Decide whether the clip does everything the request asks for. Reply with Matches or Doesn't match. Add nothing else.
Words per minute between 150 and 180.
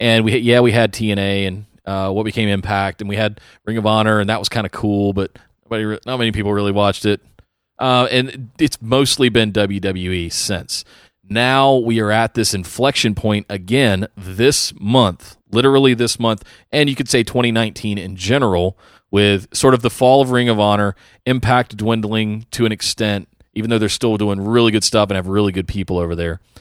Doesn't match